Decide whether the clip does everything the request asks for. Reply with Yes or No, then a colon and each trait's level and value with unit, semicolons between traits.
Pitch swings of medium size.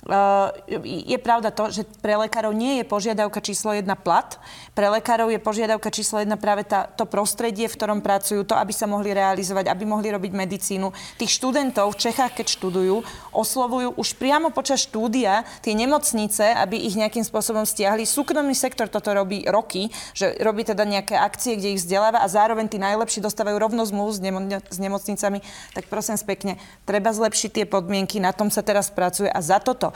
No: narrow, 2.0 semitones